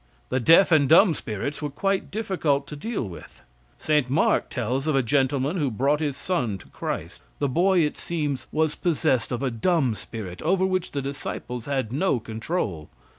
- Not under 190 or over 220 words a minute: No, average, 180 wpm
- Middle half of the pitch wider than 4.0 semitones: Yes, average, 4.7 semitones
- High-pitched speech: No, medium, 140 Hz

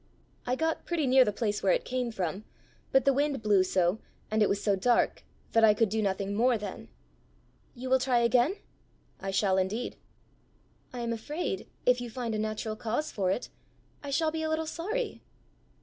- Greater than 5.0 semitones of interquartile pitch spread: No, average, 4.3 semitones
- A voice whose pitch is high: Yes, high, 235 Hz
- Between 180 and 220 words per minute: Yes, average, 190 wpm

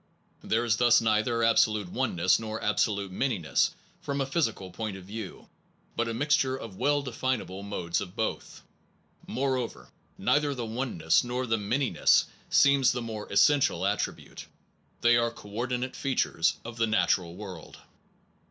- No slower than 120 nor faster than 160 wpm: Yes, average, 145 wpm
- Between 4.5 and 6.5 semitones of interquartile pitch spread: No, average, 4.1 semitones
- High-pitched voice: No, low, 115 Hz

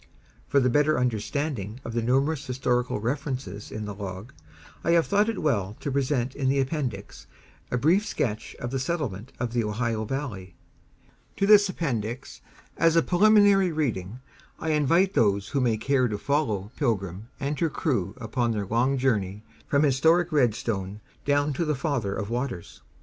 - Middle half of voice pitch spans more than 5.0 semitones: Yes, wide, 5.4 semitones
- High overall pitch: No, low, 130 Hz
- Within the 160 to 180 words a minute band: Yes, average, 165 wpm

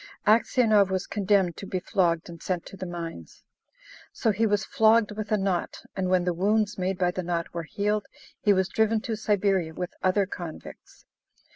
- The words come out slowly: No, average, 185 wpm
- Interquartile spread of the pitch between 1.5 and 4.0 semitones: Yes, average, 2.9 semitones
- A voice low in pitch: No, high, 190 Hz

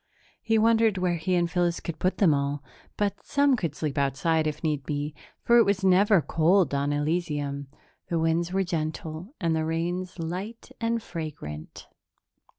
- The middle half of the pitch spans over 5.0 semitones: No, average, 3.9 semitones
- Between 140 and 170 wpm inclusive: Yes, average, 165 wpm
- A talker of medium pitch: Yes, medium, 170 Hz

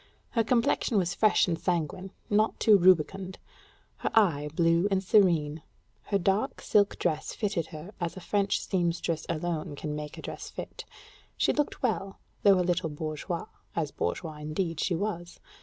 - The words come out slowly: No, average, 160 wpm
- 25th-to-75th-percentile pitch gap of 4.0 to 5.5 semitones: No, average, 3.5 semitones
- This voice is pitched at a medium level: Yes, medium, 175 Hz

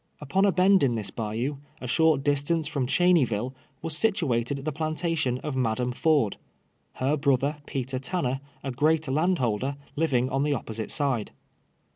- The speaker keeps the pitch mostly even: No, average, 4.0 semitones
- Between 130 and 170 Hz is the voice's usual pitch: Yes, medium, 140 Hz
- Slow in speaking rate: No, average, 160 wpm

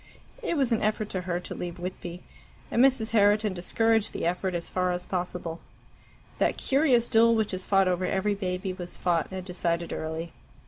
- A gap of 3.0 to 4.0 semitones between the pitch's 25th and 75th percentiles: Yes, average, 3.6 semitones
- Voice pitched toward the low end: No, medium, 185 Hz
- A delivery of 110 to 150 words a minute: No, average, 185 wpm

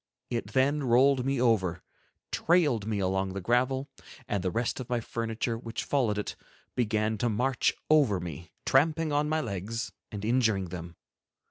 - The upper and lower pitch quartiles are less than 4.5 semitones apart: No, average, 4.8 semitones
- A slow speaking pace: No, average, 160 wpm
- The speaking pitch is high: No, low, 115 Hz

